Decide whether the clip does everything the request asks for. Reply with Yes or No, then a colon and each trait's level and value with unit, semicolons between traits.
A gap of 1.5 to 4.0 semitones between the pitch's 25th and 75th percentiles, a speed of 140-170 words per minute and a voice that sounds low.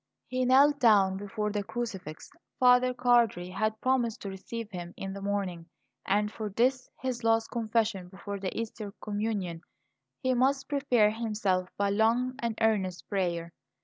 No: average, 3.7 semitones; average, 150 wpm; high, 215 Hz